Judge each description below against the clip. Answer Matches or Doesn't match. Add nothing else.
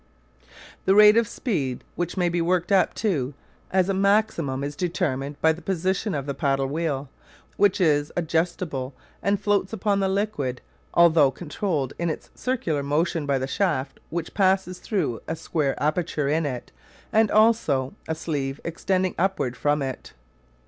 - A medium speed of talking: Matches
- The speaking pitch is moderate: Matches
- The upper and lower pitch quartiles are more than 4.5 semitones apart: Matches